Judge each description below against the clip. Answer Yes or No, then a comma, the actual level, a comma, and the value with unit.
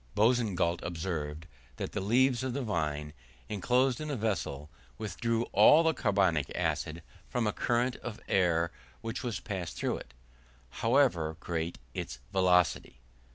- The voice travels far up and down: Yes, wide, 6.2 semitones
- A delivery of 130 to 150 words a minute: Yes, average, 140 wpm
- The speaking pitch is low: Yes, low, 100 Hz